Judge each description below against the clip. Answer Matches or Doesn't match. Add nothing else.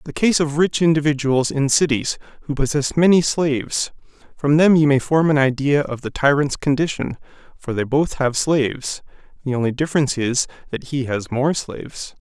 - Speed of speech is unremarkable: Matches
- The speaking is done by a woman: Doesn't match